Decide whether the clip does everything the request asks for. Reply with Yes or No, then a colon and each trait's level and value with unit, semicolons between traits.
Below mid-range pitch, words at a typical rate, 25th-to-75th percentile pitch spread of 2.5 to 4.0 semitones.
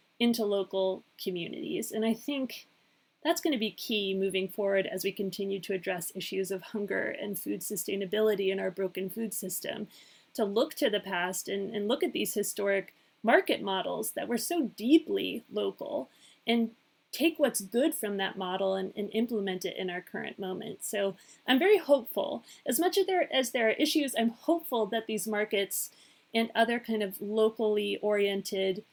No: high, 210 Hz; average, 175 wpm; average, 3.5 semitones